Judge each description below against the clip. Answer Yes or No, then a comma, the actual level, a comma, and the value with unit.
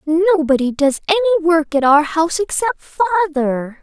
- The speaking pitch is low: No, very high, 330 Hz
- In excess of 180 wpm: No, average, 140 wpm